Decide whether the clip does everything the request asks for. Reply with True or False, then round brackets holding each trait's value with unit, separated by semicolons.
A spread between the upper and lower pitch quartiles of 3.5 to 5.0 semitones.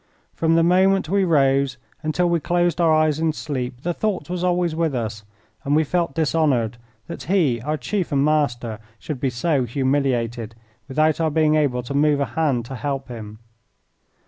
True (4.3 semitones)